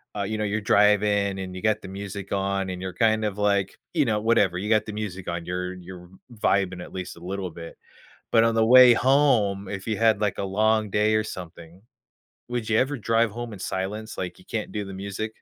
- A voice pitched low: Yes, low, 100 Hz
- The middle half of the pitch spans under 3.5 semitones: Yes, narrow, 2.6 semitones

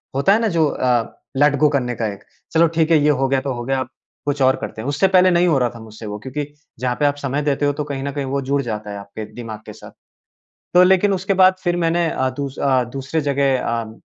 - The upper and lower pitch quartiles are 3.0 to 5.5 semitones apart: Yes, average, 4.4 semitones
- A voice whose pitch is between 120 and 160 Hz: Yes, medium, 140 Hz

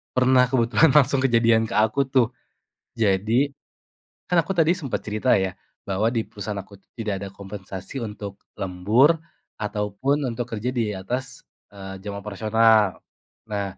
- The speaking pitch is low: Yes, low, 110 Hz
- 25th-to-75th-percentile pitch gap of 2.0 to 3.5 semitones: No, average, 4.1 semitones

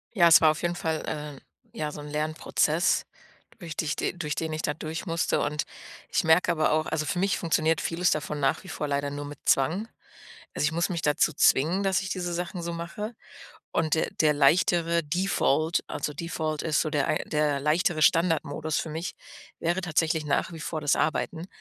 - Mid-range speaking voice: Yes, medium, 160 Hz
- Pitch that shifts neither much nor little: No, narrow, 2.1 semitones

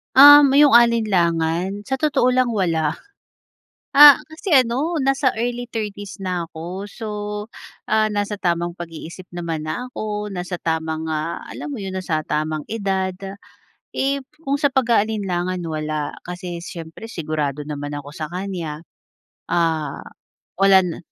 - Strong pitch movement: Yes, wide, 6.3 semitones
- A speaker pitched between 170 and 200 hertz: Yes, medium, 185 Hz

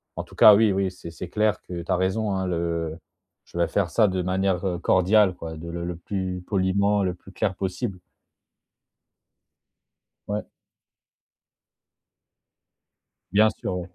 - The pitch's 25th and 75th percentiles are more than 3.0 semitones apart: No, narrow, 2.4 semitones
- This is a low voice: Yes, very low, 95 Hz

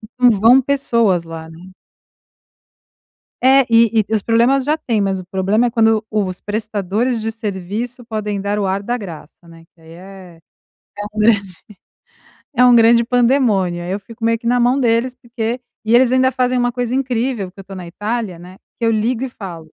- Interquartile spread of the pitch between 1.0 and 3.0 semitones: No, average, 4.1 semitones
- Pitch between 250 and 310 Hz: No, high, 220 Hz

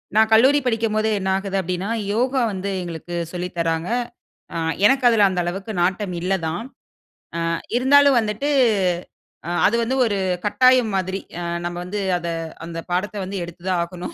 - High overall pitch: Yes, high, 195 Hz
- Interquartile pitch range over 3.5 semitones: Yes, average, 4.2 semitones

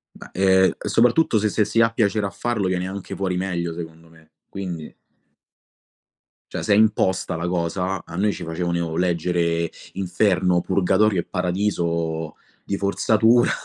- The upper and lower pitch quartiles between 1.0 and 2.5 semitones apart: No, average, 2.9 semitones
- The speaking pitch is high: No, very low, 90 Hz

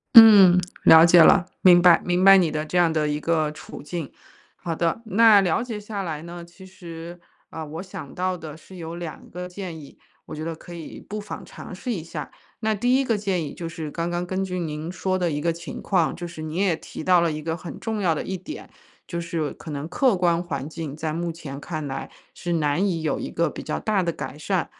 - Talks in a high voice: No, medium, 170 Hz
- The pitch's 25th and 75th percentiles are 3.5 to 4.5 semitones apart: No, average, 2.8 semitones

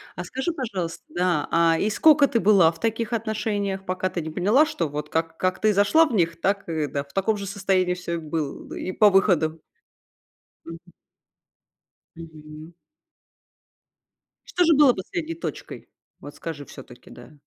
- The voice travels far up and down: No, average, 4.8 semitones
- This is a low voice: No, medium, 185 Hz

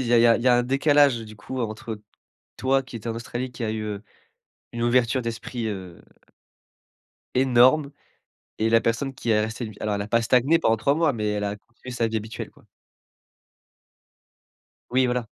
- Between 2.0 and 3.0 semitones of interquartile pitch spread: Yes, narrow, 2.6 semitones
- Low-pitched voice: Yes, low, 115 Hz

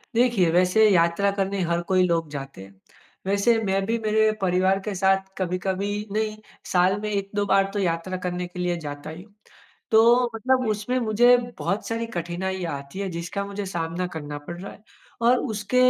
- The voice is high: Yes, high, 195 Hz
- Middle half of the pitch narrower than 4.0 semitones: Yes, average, 3.5 semitones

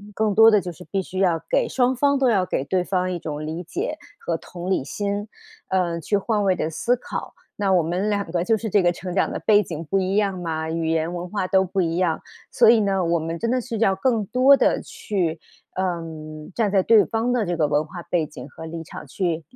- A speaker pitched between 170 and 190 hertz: Yes, medium, 185 Hz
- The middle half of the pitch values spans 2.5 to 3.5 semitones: No, average, 4.0 semitones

